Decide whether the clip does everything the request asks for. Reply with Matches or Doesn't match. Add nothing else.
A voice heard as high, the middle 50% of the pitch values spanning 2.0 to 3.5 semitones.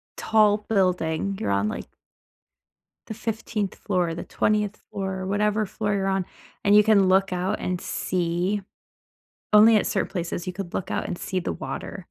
Matches